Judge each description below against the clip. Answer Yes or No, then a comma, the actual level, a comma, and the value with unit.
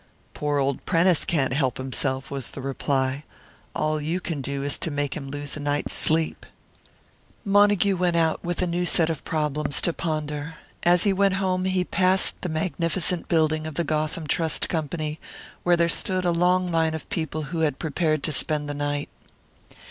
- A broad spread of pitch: No, average, 3.3 semitones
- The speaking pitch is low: No, medium, 160 Hz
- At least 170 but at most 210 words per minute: Yes, average, 185 wpm